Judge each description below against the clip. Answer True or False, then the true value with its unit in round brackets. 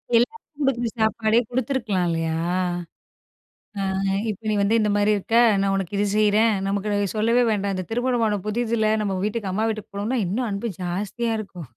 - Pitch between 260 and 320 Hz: False (215 Hz)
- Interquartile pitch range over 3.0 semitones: False (2.6 semitones)